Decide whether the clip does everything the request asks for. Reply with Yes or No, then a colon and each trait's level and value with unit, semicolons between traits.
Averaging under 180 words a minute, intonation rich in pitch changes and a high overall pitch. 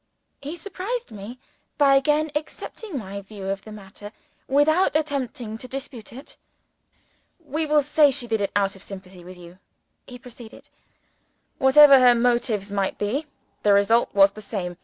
Yes: average, 160 wpm; wide, 6.3 semitones; high, 240 Hz